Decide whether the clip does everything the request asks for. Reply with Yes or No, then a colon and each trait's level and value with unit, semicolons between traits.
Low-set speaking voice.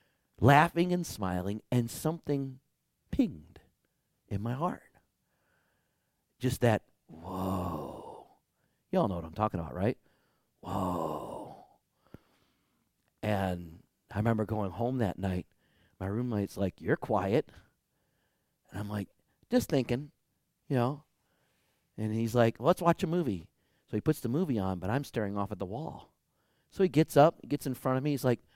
Yes: low, 115 Hz